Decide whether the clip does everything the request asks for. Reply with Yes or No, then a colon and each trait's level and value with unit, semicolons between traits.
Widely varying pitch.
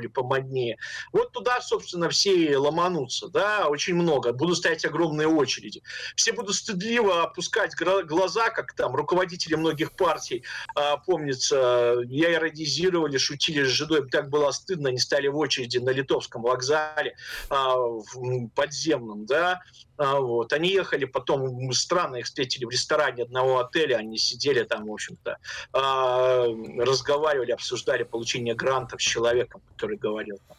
Yes: wide, 5.9 semitones